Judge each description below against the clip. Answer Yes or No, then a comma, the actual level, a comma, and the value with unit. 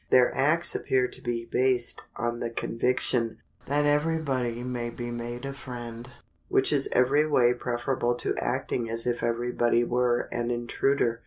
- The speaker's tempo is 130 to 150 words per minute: No, average, 165 wpm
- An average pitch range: No, narrow, 1.7 semitones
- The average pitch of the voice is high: No, low, 120 Hz